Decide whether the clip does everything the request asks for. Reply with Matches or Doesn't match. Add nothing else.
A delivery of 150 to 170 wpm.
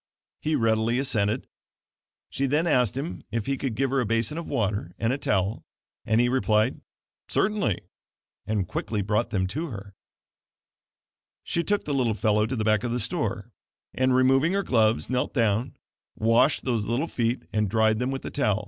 Doesn't match